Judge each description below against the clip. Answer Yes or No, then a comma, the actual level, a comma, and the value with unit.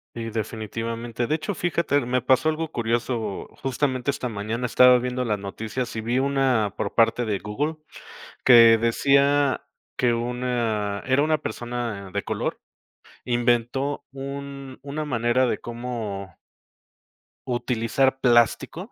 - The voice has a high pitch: No, low, 120 Hz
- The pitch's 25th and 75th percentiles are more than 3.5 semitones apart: No, average, 2.9 semitones